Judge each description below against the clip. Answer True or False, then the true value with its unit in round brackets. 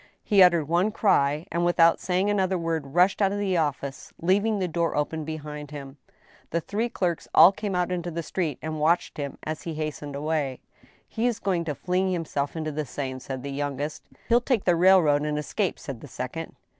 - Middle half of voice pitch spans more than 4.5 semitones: False (3.9 semitones)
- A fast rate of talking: True (210 wpm)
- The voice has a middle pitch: True (165 Hz)